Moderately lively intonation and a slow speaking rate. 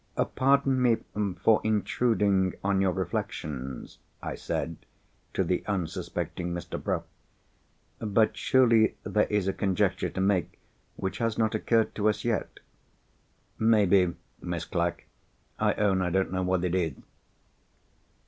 Yes: average, 3.4 semitones; slow, 130 wpm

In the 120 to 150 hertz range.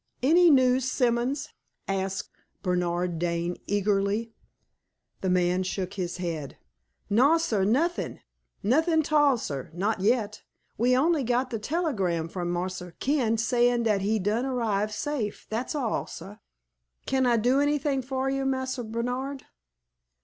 No: high, 230 Hz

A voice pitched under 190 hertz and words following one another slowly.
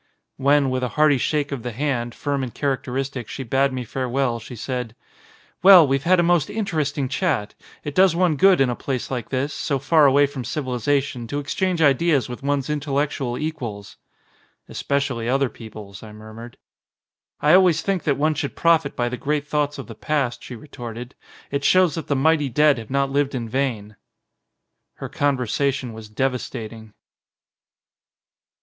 No: low, 135 Hz; average, 170 wpm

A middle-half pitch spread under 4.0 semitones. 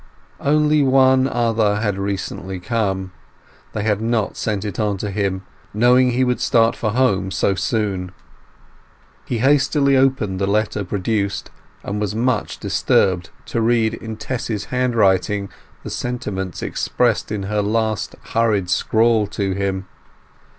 Yes: average, 3.3 semitones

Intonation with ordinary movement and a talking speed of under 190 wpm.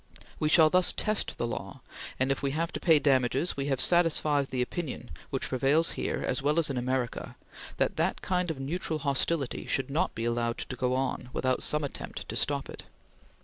No: average, 3.7 semitones; average, 200 wpm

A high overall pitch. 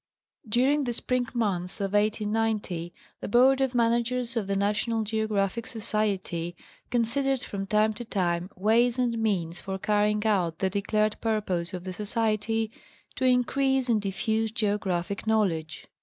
Yes: high, 215 Hz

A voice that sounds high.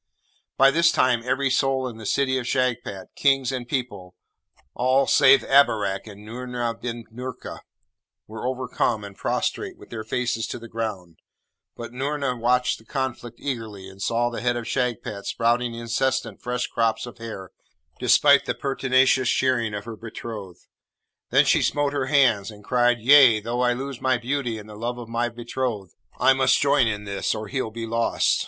No: low, 120 Hz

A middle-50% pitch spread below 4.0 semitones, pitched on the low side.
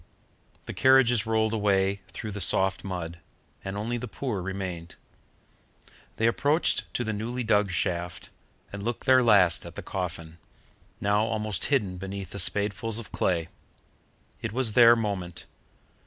Yes: average, 3.4 semitones; low, 105 Hz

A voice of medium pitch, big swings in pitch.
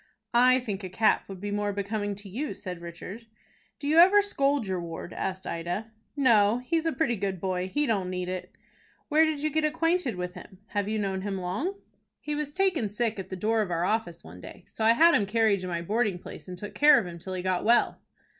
No: high, 205 Hz; wide, 6.4 semitones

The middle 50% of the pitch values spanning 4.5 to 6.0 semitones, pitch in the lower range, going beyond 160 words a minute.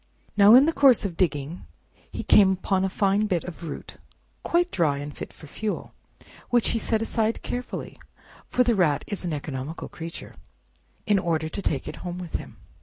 No: average, 5.2 semitones; medium, 185 Hz; average, 180 wpm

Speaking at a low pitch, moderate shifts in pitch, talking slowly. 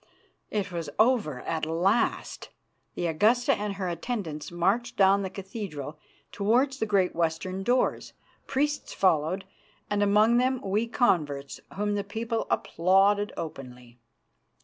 No: high, 195 Hz; average, 5.0 semitones; slow, 125 wpm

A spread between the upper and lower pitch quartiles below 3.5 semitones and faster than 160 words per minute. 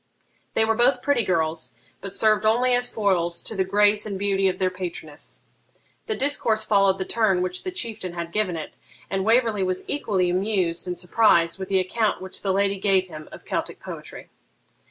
Yes: average, 3.1 semitones; average, 190 wpm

